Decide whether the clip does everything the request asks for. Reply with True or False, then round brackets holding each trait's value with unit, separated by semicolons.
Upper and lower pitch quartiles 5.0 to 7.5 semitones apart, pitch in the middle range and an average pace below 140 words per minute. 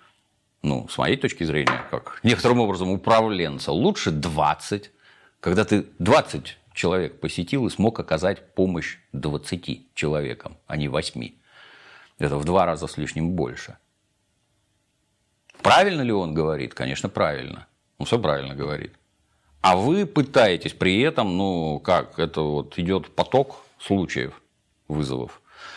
False (5.6 semitones; 85 Hz; 130 wpm)